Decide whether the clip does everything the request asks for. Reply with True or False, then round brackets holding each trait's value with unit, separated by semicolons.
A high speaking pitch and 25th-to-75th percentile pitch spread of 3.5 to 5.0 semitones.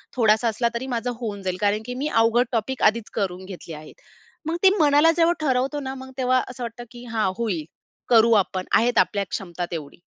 True (230 Hz; 4.2 semitones)